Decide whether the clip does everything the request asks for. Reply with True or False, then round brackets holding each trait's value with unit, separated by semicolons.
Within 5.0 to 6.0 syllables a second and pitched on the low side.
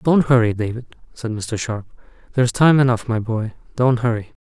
True (5.5 syllables/s; 120 Hz)